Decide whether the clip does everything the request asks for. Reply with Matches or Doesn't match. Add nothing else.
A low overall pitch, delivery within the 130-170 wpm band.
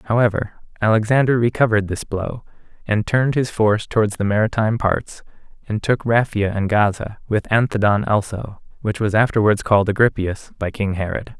Matches